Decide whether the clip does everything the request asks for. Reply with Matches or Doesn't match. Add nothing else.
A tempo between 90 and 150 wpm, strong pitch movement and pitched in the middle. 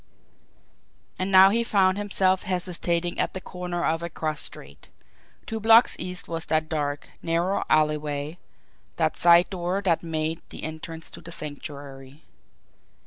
Doesn't match